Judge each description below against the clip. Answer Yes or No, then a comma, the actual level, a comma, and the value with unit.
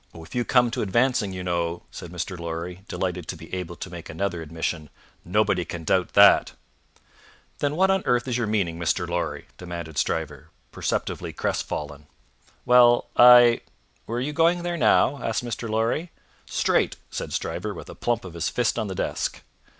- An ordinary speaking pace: Yes, average, 175 wpm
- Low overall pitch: Yes, very low, 95 Hz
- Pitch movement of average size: No, wide, 6.3 semitones